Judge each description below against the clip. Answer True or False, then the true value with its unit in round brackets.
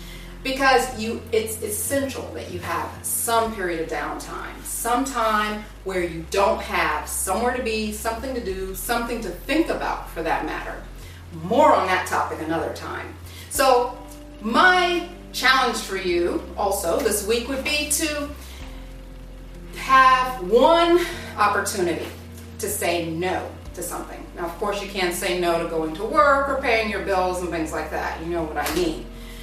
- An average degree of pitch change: False (7.3 semitones)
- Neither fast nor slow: True (160 wpm)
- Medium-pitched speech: False (205 Hz)